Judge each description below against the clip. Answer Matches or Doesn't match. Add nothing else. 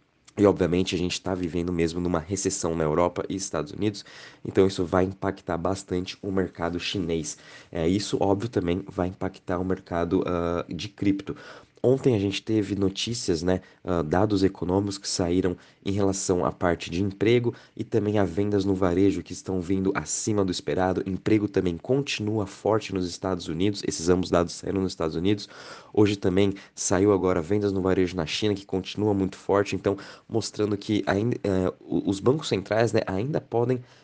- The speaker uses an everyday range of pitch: Doesn't match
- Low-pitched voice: Matches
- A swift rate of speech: Doesn't match